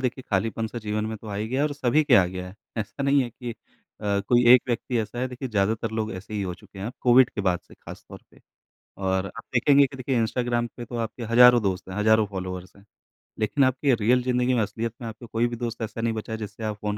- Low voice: Yes, low, 115 Hz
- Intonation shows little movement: No, average, 3.0 semitones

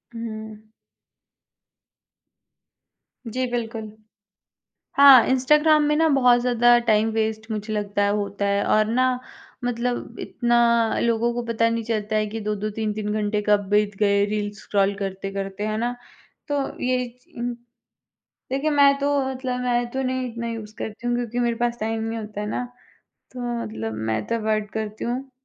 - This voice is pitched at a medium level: No, high, 225 Hz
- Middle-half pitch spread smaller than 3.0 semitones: Yes, narrow, 2.5 semitones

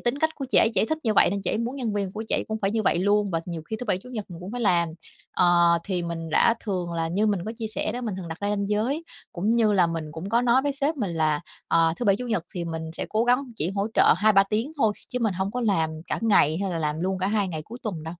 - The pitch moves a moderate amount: Yes, average, 4.7 semitones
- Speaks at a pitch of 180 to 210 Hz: Yes, high, 200 Hz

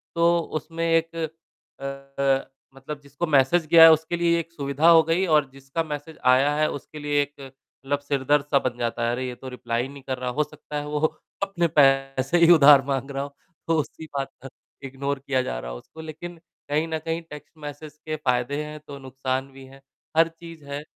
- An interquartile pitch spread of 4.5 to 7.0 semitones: No, average, 2.9 semitones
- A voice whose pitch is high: No, medium, 145 Hz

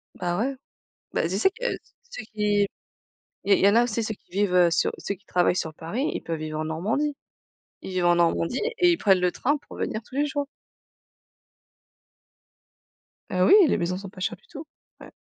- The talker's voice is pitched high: Yes, high, 200 Hz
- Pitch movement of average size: No, wide, 6.6 semitones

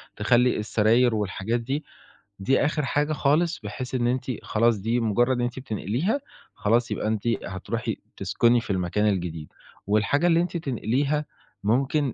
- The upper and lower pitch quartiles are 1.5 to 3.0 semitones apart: No, average, 4.6 semitones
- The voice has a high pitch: No, low, 120 Hz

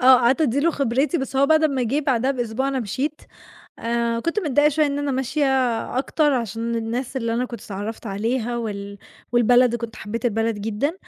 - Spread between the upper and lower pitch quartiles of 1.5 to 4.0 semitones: Yes, average, 3.4 semitones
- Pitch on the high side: Yes, high, 245 Hz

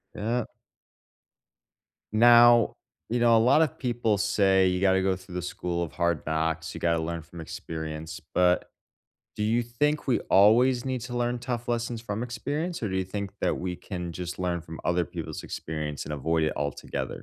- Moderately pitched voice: No, very low, 95 Hz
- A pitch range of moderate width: No, wide, 5.8 semitones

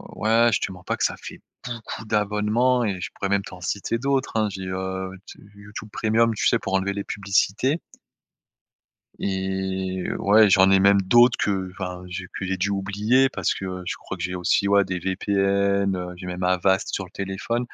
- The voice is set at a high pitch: No, low, 100 Hz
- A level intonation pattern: Yes, narrow, 2.1 semitones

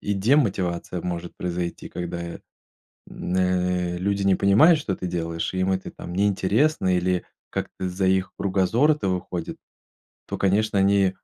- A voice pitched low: Yes, very low, 95 Hz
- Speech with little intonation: Yes, narrow, 1.9 semitones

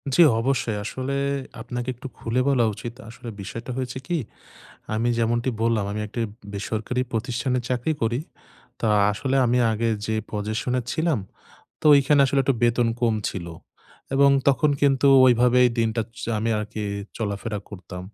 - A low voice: Yes, low, 120 Hz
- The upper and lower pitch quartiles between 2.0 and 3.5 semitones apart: Yes, narrow, 2.6 semitones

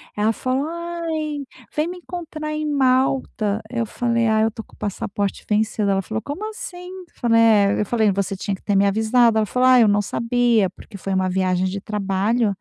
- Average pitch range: Yes, average, 4.8 semitones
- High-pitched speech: Yes, high, 225 Hz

